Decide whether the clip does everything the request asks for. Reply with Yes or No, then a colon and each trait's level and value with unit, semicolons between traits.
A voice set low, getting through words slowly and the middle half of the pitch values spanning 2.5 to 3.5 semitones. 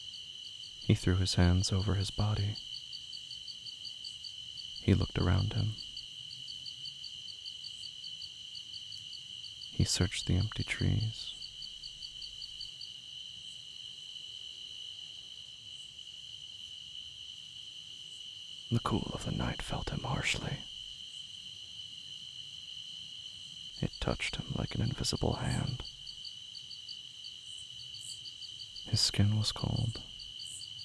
Yes: low, 110 Hz; slow, 70 wpm; average, 3.0 semitones